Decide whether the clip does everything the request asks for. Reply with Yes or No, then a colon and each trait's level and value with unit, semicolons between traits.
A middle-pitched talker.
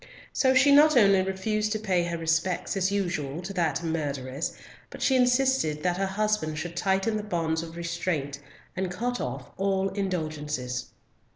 Yes: medium, 180 Hz